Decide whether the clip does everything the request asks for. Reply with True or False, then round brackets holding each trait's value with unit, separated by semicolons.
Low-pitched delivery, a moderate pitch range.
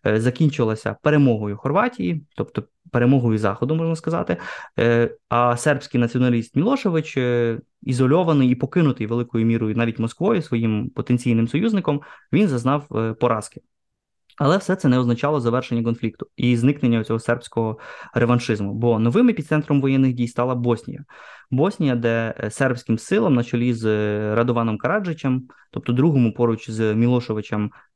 True (120 Hz; 3.6 semitones)